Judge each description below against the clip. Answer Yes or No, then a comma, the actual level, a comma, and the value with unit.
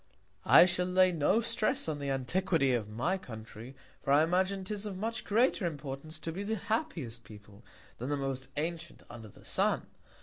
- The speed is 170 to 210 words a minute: Yes, average, 180 wpm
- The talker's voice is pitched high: No, medium, 160 Hz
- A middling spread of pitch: No, wide, 6.3 semitones